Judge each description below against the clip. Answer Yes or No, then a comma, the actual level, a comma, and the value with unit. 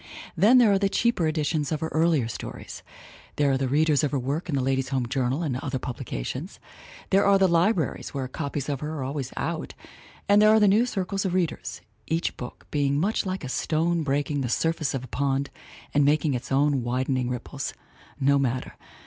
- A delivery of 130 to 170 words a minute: No, average, 200 wpm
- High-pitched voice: No, medium, 145 Hz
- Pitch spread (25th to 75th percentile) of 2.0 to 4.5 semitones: Yes, average, 4.2 semitones